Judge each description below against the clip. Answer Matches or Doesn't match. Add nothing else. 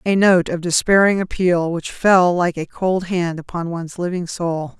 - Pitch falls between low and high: Matches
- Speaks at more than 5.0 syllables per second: Doesn't match